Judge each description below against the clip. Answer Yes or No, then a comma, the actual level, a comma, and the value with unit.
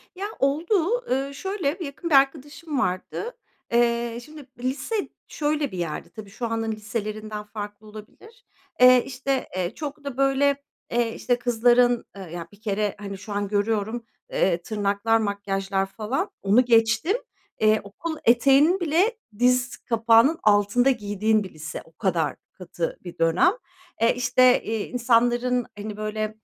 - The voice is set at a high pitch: Yes, high, 230 Hz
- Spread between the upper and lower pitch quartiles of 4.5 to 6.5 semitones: Yes, average, 4.8 semitones